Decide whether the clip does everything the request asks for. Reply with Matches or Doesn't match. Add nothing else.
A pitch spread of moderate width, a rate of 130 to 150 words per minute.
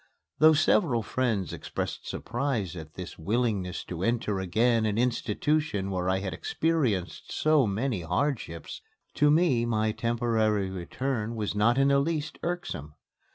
Doesn't match